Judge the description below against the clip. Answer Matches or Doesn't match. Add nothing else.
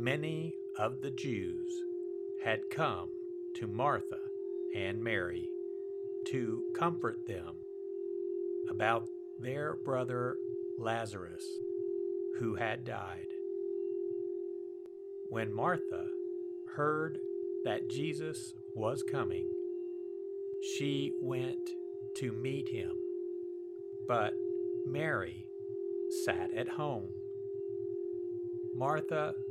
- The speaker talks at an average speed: Doesn't match